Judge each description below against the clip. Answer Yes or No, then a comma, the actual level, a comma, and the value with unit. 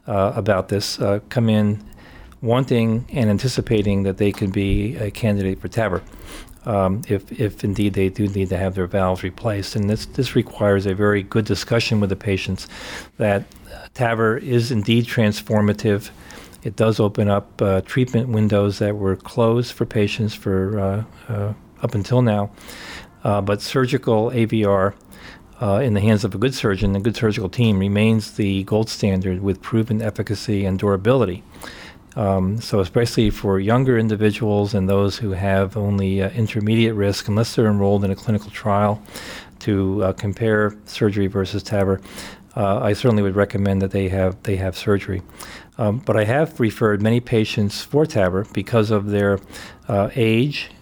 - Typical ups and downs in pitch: No, narrow, 2.2 semitones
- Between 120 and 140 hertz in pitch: No, low, 105 Hz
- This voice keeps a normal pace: Yes, average, 165 wpm